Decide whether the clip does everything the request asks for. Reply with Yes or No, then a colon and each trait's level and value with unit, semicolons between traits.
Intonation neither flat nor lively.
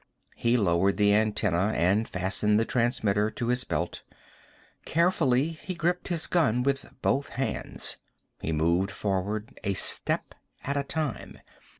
No: wide, 5.8 semitones